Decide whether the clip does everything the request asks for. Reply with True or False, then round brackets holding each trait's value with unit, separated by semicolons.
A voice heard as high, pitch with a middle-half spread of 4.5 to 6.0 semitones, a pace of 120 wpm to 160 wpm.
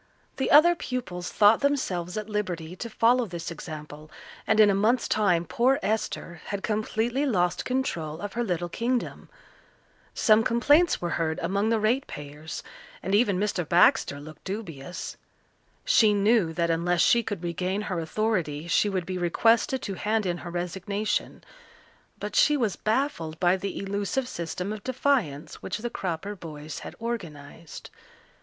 True (200 Hz; 5.0 semitones; 155 wpm)